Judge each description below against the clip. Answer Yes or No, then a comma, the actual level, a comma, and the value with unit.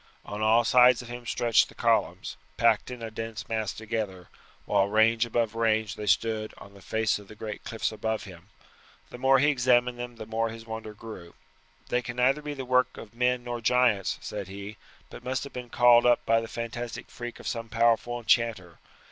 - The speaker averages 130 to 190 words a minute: No, fast, 205 wpm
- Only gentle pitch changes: Yes, narrow, 2.1 semitones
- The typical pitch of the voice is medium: No, low, 115 Hz